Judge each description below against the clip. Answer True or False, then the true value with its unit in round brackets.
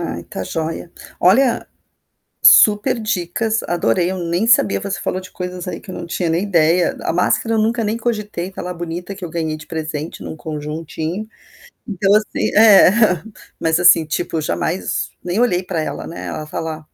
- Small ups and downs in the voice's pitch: False (4.1 semitones)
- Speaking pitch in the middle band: True (175 Hz)